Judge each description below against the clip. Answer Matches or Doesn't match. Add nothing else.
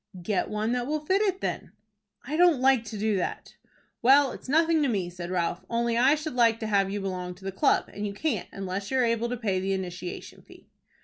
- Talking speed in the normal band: Doesn't match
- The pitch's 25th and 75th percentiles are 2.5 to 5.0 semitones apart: Doesn't match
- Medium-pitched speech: Doesn't match